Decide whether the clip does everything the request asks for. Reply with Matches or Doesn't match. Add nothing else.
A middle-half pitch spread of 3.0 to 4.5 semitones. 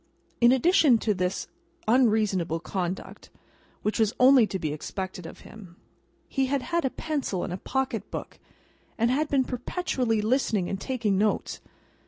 Doesn't match